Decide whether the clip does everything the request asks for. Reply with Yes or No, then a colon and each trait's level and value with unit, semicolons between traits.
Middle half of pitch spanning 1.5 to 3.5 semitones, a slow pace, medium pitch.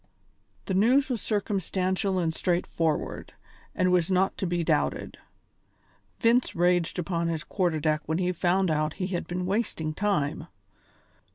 No: average, 2.9 semitones; average, 150 wpm; medium, 180 Hz